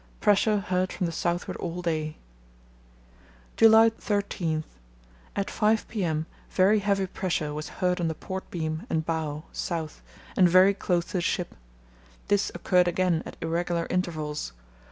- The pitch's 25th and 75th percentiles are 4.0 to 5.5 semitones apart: No, average, 3.3 semitones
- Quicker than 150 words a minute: No, average, 140 wpm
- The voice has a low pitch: No, medium, 175 Hz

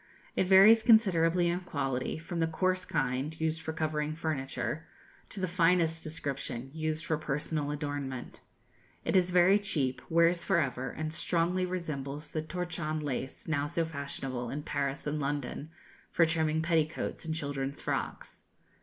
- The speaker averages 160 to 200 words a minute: No, average, 150 wpm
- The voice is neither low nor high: Yes, medium, 160 Hz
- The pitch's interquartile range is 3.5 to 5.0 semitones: No, average, 3.1 semitones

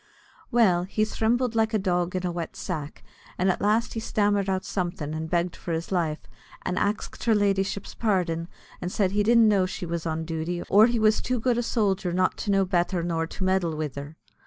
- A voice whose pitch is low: No, medium, 185 Hz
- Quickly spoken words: Yes, fast, 215 wpm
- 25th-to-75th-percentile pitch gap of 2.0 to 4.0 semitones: Yes, average, 3.7 semitones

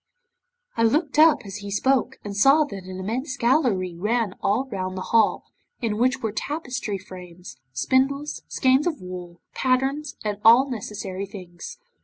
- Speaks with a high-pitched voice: Yes, high, 225 Hz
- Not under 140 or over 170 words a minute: Yes, average, 155 wpm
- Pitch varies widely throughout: Yes, wide, 6.0 semitones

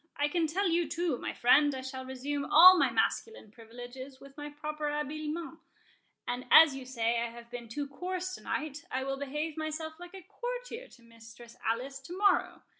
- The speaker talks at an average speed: Yes, average, 190 wpm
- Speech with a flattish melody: No, average, 4.3 semitones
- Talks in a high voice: Yes, very high, 290 Hz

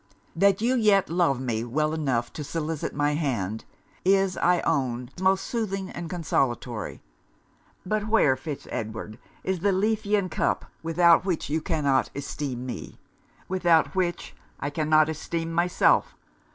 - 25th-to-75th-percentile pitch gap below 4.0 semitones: No, wide, 5.5 semitones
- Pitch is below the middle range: No, medium, 160 Hz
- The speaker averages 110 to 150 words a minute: Yes, average, 140 wpm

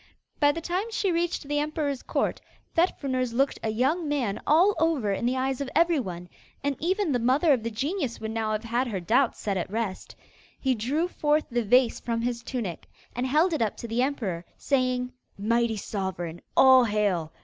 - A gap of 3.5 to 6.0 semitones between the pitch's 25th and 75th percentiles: Yes, average, 5.0 semitones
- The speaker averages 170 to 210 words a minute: Yes, average, 195 wpm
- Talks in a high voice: Yes, very high, 255 Hz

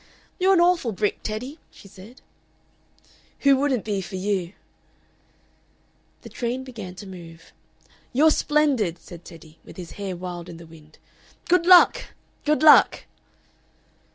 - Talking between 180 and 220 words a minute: No, slow, 135 wpm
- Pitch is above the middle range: Yes, high, 210 Hz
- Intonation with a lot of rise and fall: Yes, wide, 8.1 semitones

